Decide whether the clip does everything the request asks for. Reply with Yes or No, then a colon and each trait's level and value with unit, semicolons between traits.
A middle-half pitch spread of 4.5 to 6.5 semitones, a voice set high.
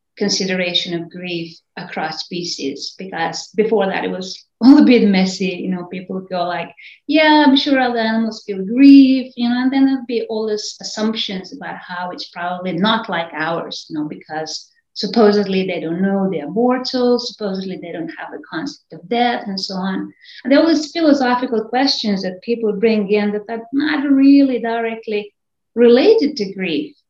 Yes: average, 5.2 semitones; high, 210 Hz